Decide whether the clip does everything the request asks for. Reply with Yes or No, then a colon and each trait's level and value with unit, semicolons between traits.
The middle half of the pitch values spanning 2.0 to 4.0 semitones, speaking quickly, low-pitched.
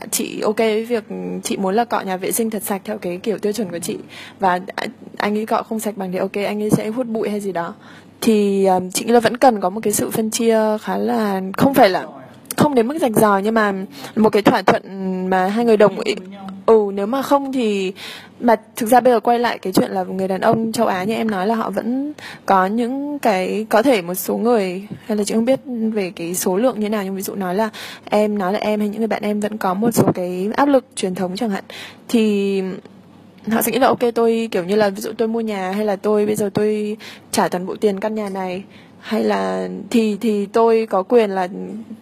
No: average, 2.9 semitones; fast, 255 wpm; high, 215 Hz